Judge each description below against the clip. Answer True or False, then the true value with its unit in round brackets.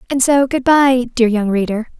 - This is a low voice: False (245 Hz)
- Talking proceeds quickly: True (210 wpm)